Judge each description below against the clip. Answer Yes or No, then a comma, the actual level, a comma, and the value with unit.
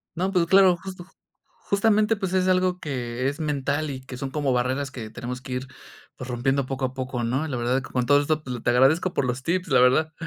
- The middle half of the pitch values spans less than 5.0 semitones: No, wide, 5.4 semitones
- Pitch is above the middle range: No, low, 135 Hz